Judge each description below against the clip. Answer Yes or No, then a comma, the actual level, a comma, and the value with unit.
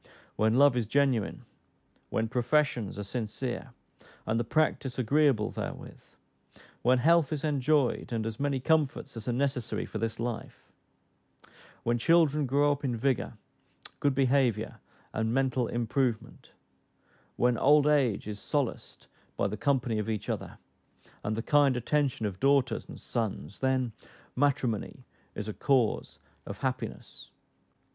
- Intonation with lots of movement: No, average, 3.9 semitones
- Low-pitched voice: Yes, low, 125 Hz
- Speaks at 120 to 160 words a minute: Yes, slow, 135 wpm